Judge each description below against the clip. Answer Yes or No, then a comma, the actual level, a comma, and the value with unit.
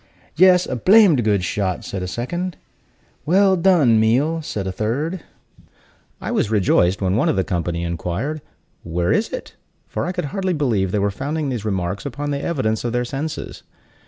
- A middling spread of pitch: No, wide, 8.5 semitones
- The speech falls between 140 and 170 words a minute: No, average, 180 wpm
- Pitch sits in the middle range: No, low, 120 Hz